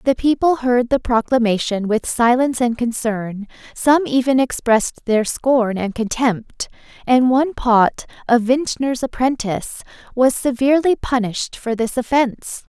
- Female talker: Yes, female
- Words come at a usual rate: No, slow, 130 wpm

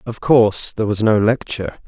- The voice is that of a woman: No, male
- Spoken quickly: No, average, 190 wpm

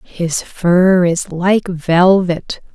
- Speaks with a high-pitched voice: No, medium, 175 Hz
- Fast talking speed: No, slow, 110 wpm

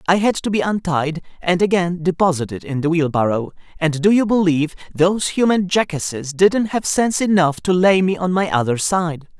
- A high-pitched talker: No, medium, 175 Hz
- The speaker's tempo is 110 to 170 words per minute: No, average, 185 wpm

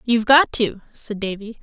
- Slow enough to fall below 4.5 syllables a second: No, 5.0 syllables/s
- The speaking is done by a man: No, female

